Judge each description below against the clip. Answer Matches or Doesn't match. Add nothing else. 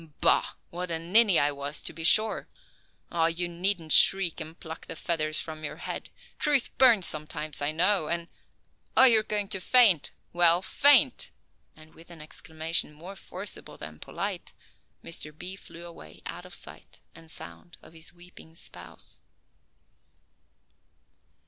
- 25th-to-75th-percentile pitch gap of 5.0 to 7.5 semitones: Doesn't match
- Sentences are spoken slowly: Doesn't match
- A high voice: Doesn't match